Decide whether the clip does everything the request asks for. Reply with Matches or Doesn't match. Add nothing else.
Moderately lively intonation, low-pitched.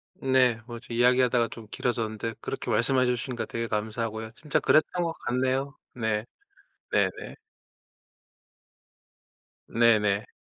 Doesn't match